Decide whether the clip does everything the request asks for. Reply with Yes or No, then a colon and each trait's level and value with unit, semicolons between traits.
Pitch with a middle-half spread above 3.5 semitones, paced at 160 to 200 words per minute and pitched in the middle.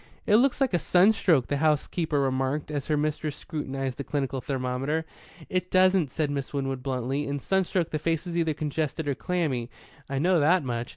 Yes: average, 3.9 semitones; average, 185 wpm; medium, 150 Hz